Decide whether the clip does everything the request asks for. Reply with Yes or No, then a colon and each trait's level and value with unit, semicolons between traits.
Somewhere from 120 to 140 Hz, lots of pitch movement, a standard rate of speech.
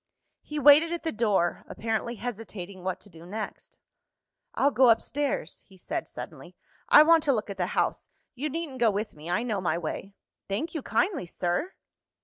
No: high, 225 Hz; wide, 7.3 semitones; average, 180 wpm